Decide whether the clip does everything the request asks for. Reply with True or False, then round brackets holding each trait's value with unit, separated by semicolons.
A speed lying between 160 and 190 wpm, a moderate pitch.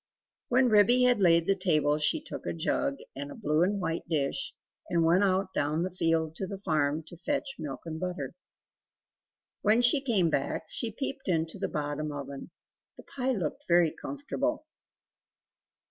True (170 wpm; 175 Hz)